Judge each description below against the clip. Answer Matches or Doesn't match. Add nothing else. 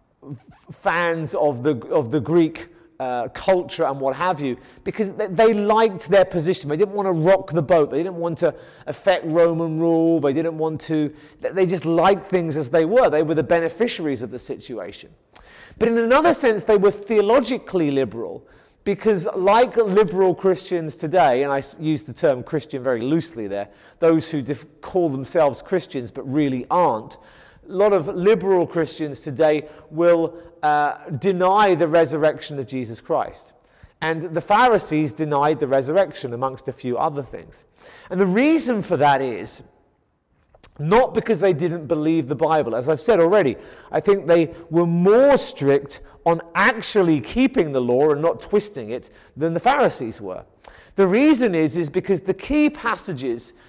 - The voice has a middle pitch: Matches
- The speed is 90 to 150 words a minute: Doesn't match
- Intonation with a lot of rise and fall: Doesn't match